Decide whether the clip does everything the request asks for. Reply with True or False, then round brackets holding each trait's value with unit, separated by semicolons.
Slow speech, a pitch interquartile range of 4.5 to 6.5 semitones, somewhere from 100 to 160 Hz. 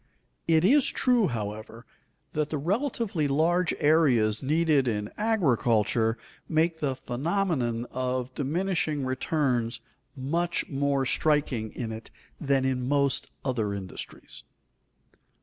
True (110 wpm; 5.2 semitones; 140 Hz)